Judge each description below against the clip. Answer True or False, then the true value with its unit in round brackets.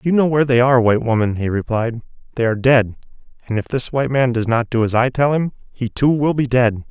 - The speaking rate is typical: False (250 wpm)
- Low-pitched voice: True (125 Hz)